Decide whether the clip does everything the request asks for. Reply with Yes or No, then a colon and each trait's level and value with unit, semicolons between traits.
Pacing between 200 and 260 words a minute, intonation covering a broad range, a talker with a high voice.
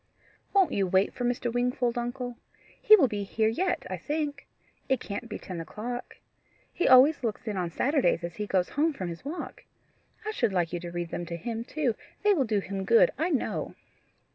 Yes: fast, 205 wpm; wide, 6.9 semitones; high, 240 Hz